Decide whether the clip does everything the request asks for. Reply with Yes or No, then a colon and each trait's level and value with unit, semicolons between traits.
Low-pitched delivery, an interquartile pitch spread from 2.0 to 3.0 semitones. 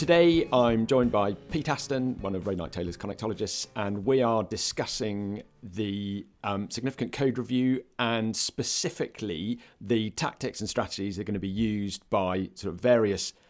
No: low, 110 Hz; average, 3.7 semitones